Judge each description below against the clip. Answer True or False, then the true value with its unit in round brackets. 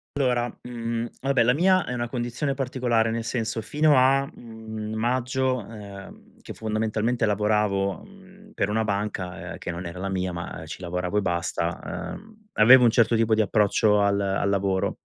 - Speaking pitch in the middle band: False (110 Hz)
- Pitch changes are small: False (3.9 semitones)